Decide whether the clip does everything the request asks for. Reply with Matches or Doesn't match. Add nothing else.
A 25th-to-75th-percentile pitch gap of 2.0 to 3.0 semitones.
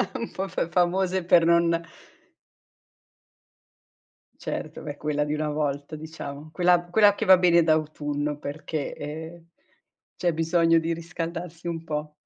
Matches